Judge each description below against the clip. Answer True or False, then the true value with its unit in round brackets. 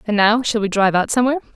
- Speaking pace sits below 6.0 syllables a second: False (8.5 syllables/s)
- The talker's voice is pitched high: True (220 Hz)